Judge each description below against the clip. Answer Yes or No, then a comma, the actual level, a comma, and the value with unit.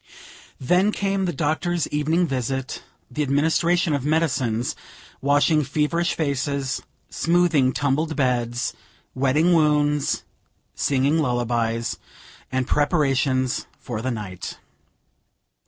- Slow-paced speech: Yes, slow, 95 wpm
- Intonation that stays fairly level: No, average, 3.7 semitones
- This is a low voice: No, medium, 145 Hz